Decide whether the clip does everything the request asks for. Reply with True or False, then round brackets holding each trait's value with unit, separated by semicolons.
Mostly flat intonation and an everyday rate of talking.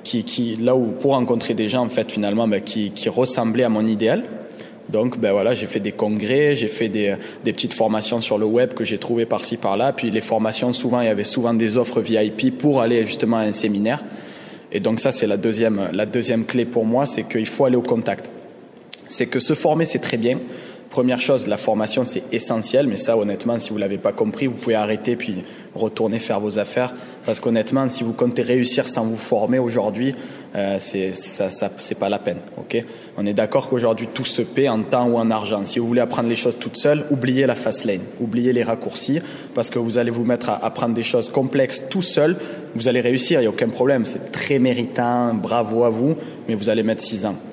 False (2.3 semitones; 230 wpm)